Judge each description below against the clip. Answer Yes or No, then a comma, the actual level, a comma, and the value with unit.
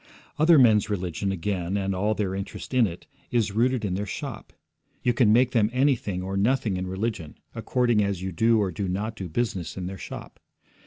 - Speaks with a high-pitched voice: No, low, 105 Hz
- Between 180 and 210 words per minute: Yes, average, 200 wpm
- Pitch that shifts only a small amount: No, average, 3.7 semitones